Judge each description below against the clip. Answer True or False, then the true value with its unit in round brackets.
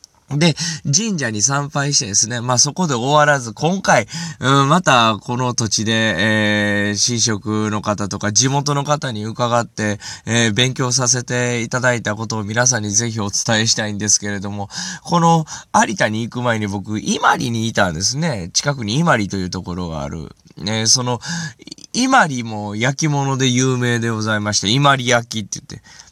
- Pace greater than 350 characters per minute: False (340 characters per minute)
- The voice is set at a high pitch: False (120 Hz)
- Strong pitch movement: False (4.9 semitones)